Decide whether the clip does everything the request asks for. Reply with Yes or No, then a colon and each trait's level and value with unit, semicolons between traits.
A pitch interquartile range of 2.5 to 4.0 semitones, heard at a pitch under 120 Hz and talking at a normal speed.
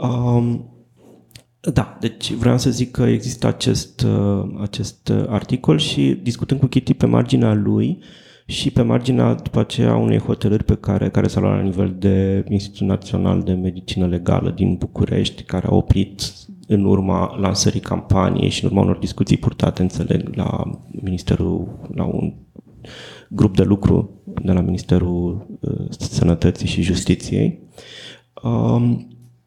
Yes: average, 3.5 semitones; low, 100 Hz; average, 140 wpm